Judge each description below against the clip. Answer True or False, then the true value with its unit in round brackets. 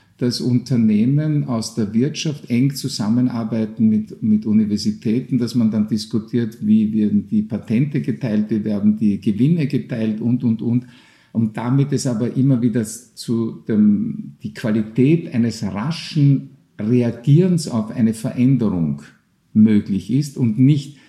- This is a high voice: False (120 Hz)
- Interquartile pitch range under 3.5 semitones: False (3.8 semitones)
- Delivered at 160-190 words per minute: False (135 wpm)